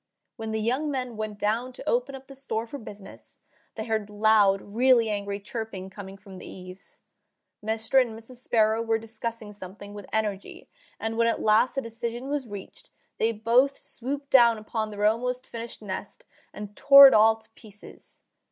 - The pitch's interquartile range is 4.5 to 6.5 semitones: No, narrow, 2.6 semitones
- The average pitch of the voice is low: No, high, 225 Hz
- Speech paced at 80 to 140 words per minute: No, average, 180 wpm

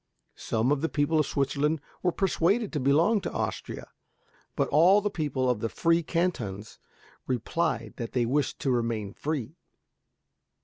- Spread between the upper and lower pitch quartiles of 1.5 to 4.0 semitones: No, wide, 5.4 semitones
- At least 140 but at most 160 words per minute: Yes, average, 150 wpm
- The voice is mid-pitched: Yes, medium, 145 Hz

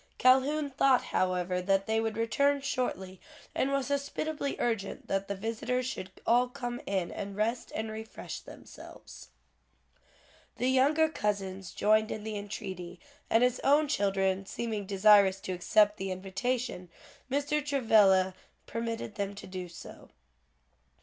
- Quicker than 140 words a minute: No, slow, 135 wpm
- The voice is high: Yes, high, 220 Hz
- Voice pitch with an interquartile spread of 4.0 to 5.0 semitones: Yes, average, 4.7 semitones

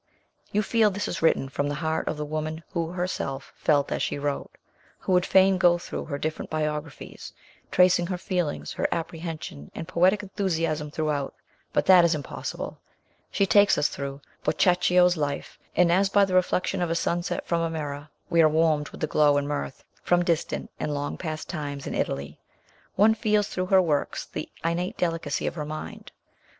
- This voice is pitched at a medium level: Yes, medium, 165 Hz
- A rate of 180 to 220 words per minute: Yes, average, 185 wpm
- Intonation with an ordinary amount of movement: Yes, average, 3.3 semitones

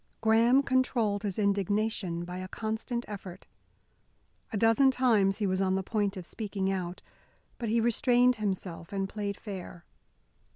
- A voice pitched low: No, high, 205 Hz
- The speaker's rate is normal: Yes, average, 150 wpm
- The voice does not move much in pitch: No, average, 3.0 semitones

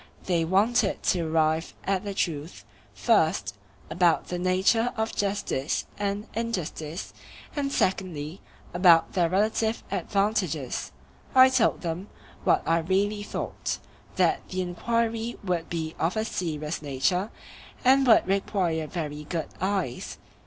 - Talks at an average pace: No, slow, 125 wpm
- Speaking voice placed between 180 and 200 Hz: Yes, medium, 185 Hz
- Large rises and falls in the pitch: No, average, 4.2 semitones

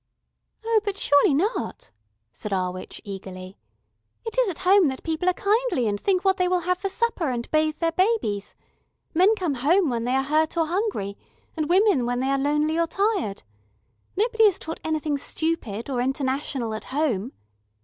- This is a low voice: No, very high, 315 Hz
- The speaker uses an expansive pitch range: Yes, wide, 7.1 semitones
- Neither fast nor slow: Yes, average, 180 wpm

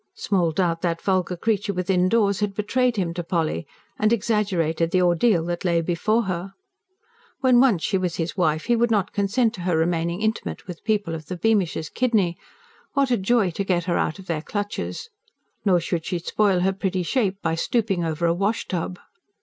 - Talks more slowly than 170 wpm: No, average, 195 wpm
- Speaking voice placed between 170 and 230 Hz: Yes, medium, 185 Hz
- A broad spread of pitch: No, average, 3.7 semitones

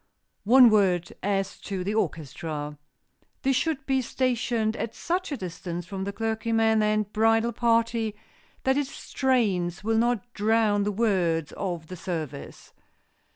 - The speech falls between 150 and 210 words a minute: No, average, 140 wpm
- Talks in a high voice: Yes, high, 215 Hz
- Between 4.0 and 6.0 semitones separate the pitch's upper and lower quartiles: Yes, average, 4.3 semitones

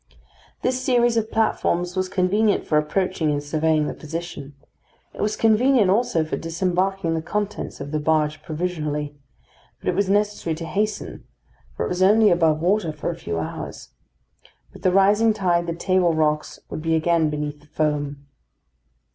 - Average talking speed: Yes, average, 165 wpm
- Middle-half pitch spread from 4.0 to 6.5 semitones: Yes, average, 4.5 semitones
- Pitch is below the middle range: No, medium, 170 Hz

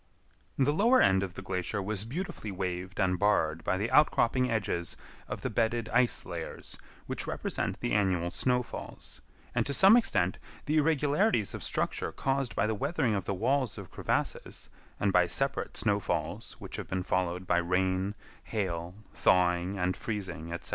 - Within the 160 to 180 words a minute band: Yes, average, 165 wpm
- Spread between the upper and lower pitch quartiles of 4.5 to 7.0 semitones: Yes, wide, 5.6 semitones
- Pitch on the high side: No, low, 100 Hz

